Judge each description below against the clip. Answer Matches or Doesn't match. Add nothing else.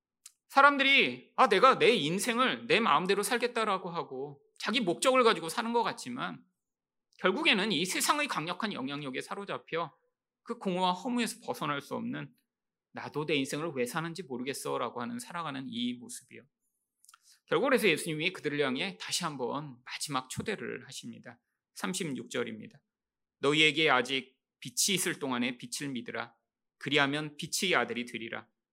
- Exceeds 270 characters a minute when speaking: Matches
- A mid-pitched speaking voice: Matches